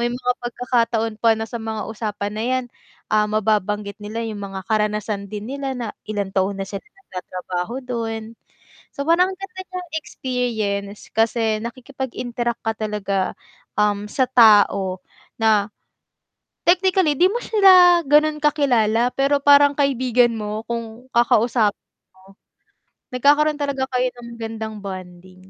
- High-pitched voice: Yes, high, 230 Hz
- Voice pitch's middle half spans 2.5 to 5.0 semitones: Yes, average, 4.2 semitones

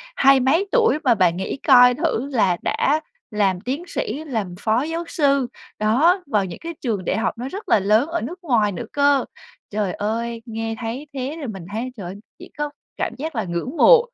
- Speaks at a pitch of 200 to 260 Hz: Yes, very high, 250 Hz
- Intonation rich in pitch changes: Yes, wide, 5.7 semitones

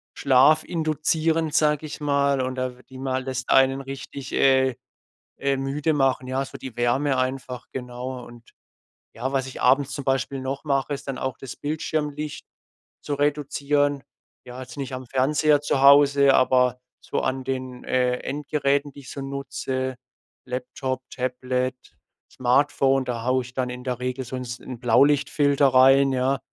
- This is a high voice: No, low, 135 Hz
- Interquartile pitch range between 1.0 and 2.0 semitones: Yes, narrow, 1.7 semitones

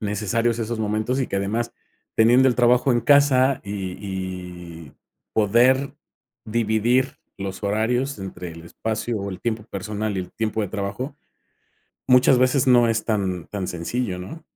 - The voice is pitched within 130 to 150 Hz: No, low, 110 Hz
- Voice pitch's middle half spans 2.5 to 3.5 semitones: No, average, 4.0 semitones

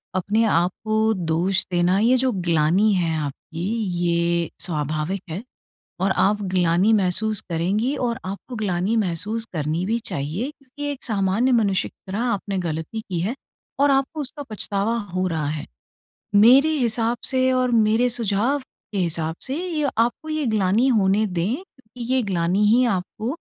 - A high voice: Yes, high, 205 Hz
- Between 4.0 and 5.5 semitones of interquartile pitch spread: Yes, average, 5.2 semitones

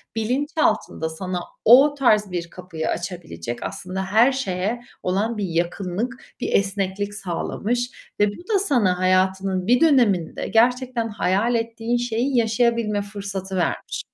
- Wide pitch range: No, average, 4.6 semitones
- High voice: Yes, high, 205 Hz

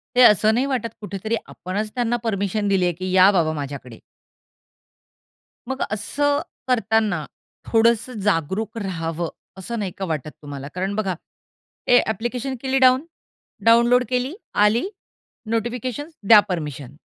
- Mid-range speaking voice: No, high, 215 Hz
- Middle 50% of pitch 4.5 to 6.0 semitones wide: Yes, average, 4.8 semitones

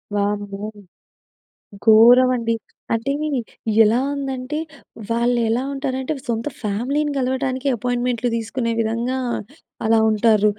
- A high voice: Yes, high, 240 Hz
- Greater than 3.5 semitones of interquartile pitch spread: No, narrow, 2.5 semitones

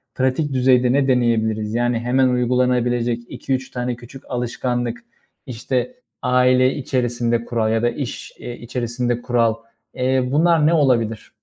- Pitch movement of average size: No, narrow, 1.5 semitones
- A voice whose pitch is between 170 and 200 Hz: No, low, 125 Hz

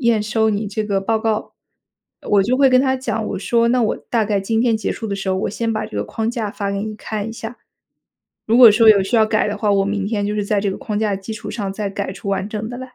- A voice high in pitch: Yes, high, 215 Hz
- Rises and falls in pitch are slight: Yes, narrow, 2.1 semitones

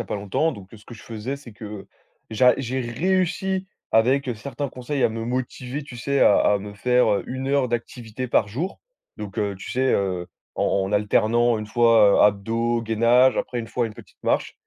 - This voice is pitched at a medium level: No, low, 120 Hz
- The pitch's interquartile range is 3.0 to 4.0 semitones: Yes, average, 3.5 semitones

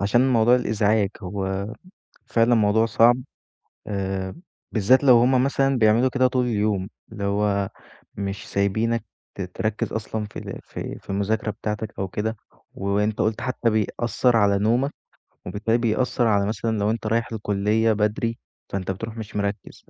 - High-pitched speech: No, low, 110 Hz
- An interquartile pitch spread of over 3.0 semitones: No, narrow, 2.4 semitones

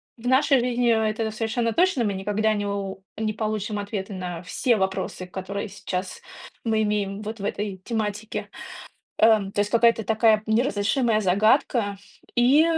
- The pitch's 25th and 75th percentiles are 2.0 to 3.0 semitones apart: Yes, narrow, 2.4 semitones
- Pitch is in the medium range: No, high, 215 Hz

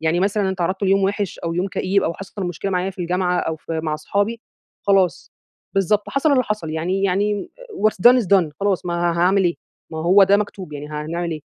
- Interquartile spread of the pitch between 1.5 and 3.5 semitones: Yes, average, 2.9 semitones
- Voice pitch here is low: No, medium, 185 Hz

